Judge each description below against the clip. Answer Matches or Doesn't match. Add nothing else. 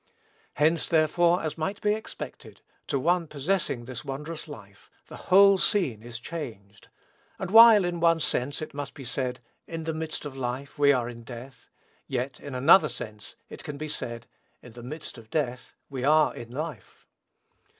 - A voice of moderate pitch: Matches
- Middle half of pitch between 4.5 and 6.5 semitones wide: Matches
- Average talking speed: Matches